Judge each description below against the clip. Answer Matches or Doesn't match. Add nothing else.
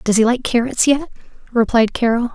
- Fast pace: Doesn't match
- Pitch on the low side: Doesn't match